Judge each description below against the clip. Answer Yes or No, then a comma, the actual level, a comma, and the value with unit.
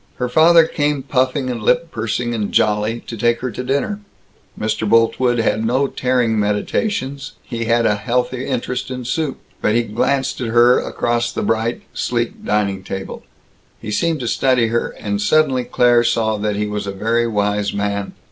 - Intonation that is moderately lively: Yes, average, 3.2 semitones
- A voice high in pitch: No, low, 120 Hz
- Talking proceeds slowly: No, average, 175 wpm